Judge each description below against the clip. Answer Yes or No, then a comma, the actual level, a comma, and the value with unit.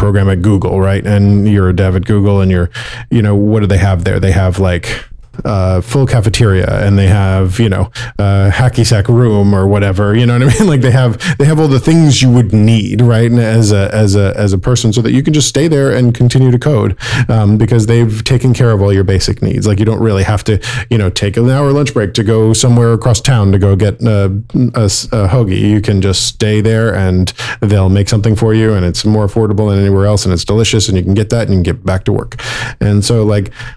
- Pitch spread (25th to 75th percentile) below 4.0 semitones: Yes, average, 3.3 semitones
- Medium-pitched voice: No, low, 110 Hz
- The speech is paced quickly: Yes, fast, 255 wpm